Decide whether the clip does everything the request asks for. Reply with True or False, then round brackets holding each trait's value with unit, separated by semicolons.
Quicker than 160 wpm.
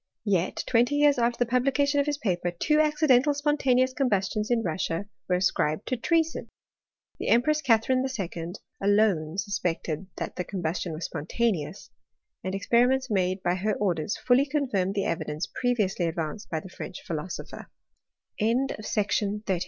False (145 wpm)